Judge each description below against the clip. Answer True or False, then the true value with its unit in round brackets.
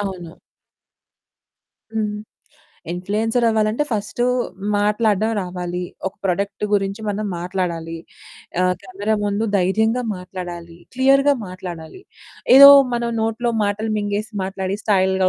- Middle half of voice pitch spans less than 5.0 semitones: True (3.1 semitones)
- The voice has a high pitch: True (200 Hz)